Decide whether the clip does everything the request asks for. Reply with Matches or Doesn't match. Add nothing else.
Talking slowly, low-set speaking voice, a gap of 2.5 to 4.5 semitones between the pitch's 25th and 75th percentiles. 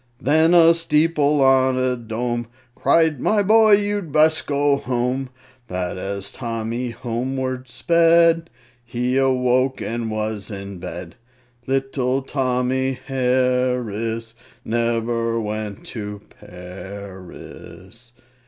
Matches